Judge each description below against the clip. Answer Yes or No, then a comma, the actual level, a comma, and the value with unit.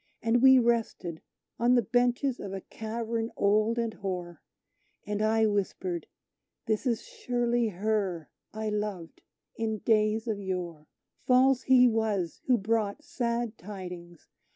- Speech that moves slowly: Yes, slow, 130 wpm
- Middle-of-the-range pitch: No, high, 220 Hz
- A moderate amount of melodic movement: Yes, average, 3.4 semitones